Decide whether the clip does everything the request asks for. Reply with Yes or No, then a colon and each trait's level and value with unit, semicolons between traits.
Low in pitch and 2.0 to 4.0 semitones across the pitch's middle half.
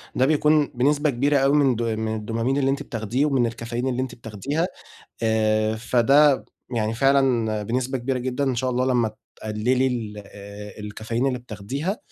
Yes: low, 125 Hz; average, 3.4 semitones